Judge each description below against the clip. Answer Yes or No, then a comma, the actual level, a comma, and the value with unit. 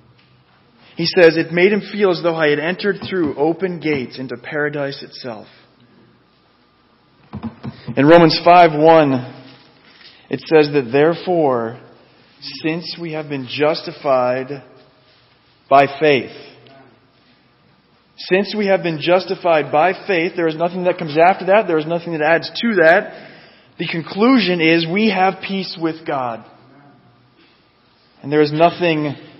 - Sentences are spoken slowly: Yes, slow, 130 wpm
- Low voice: No, medium, 160 Hz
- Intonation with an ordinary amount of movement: Yes, average, 3.8 semitones